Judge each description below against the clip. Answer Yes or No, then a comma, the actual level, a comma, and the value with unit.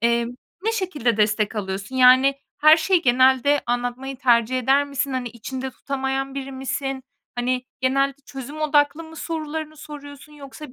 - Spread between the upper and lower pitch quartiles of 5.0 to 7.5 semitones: No, average, 2.8 semitones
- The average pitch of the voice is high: Yes, very high, 270 Hz